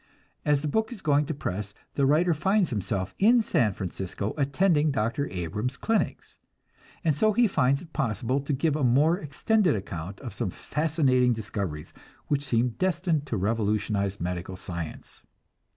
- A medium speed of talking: Yes, average, 155 wpm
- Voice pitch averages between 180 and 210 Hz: No, low, 135 Hz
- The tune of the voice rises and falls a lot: Yes, wide, 7.4 semitones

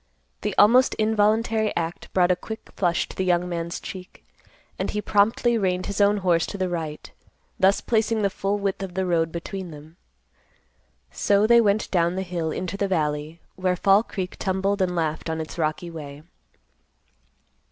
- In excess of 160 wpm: Yes, average, 175 wpm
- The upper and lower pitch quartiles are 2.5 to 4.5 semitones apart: Yes, average, 3.1 semitones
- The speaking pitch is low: No, medium, 185 Hz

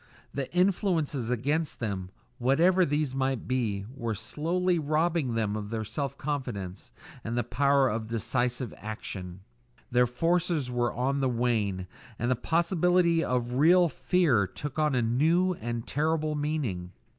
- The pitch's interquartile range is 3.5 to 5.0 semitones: No, wide, 5.5 semitones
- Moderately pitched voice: No, low, 130 Hz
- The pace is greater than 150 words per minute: No, average, 140 wpm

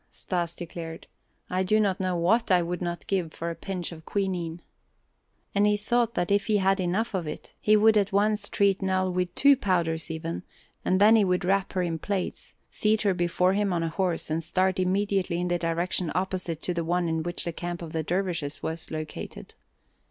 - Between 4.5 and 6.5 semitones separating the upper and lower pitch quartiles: No, average, 2.7 semitones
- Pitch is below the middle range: No, medium, 180 Hz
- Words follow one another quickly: Yes, fast, 210 wpm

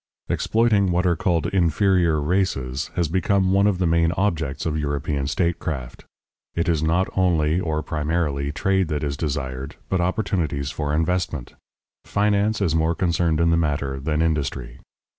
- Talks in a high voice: No, very low, 80 Hz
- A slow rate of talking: No, average, 155 wpm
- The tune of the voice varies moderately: Yes, average, 3.8 semitones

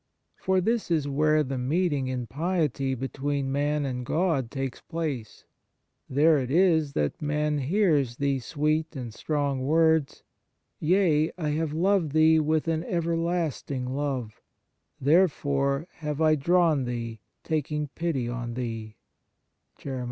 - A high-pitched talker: No, medium, 150 Hz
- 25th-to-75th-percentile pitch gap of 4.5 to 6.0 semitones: No, average, 3.3 semitones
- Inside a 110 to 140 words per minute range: Yes, slow, 135 wpm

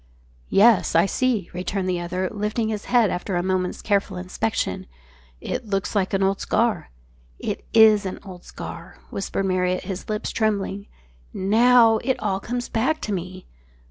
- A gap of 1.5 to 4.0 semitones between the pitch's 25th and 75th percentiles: Yes, average, 3.1 semitones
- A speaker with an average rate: Yes, average, 160 wpm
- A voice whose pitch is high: Yes, high, 200 Hz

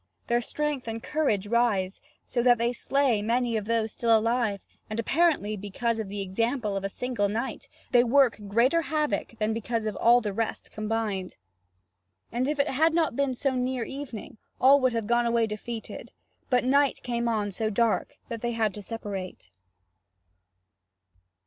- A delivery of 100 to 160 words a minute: No, average, 170 wpm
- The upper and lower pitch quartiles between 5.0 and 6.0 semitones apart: No, average, 3.0 semitones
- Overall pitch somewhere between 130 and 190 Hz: No, high, 230 Hz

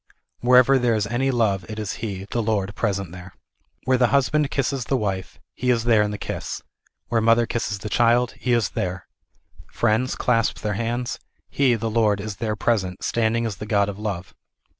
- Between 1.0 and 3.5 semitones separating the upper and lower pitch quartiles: Yes, average, 2.9 semitones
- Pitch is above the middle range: No, low, 115 Hz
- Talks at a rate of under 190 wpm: No, fast, 205 wpm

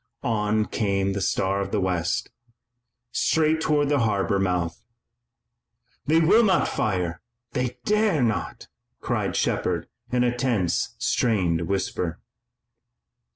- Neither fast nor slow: No, slow, 115 wpm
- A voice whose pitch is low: Yes, low, 105 Hz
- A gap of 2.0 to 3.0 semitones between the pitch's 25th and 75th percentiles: No, wide, 5.6 semitones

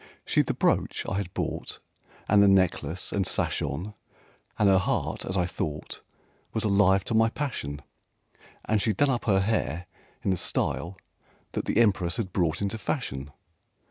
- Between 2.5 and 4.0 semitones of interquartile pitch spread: Yes, average, 3.4 semitones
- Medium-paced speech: Yes, average, 170 wpm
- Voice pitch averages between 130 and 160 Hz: No, very low, 95 Hz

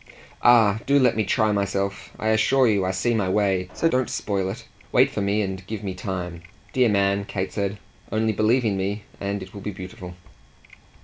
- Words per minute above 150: Yes, average, 200 wpm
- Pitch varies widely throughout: No, narrow, 2.4 semitones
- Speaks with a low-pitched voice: Yes, low, 100 Hz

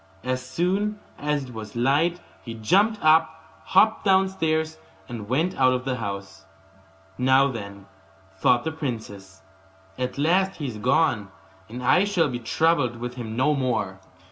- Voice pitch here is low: Yes, low, 130 Hz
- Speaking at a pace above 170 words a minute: No, average, 150 wpm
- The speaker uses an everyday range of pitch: No, wide, 5.7 semitones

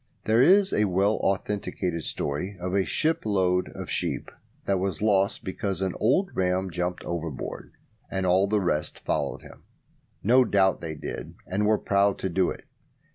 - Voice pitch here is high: No, very low, 95 Hz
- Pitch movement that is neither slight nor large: No, narrow, 2.3 semitones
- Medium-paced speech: Yes, average, 170 wpm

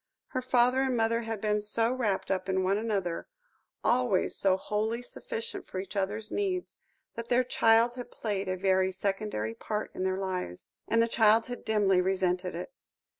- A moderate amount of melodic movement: Yes, average, 3.9 semitones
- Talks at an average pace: Yes, average, 175 wpm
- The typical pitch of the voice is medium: No, high, 210 Hz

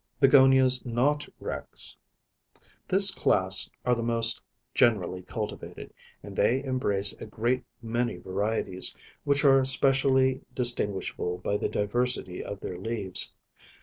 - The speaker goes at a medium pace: No, slow, 115 wpm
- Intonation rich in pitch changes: No, average, 4.5 semitones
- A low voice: Yes, low, 120 Hz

